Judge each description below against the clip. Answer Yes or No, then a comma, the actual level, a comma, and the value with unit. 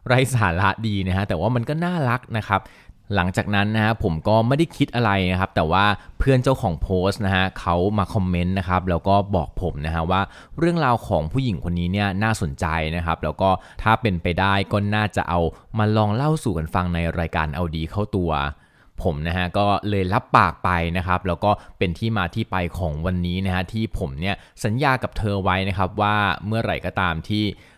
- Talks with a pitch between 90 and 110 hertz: Yes, very low, 95 Hz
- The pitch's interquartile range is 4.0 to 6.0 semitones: No, average, 3.3 semitones